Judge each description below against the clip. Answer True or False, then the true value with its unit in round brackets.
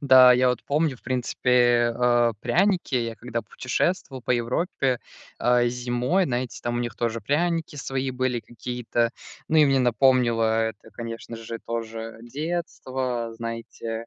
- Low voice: True (125 Hz)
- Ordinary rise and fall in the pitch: False (2.1 semitones)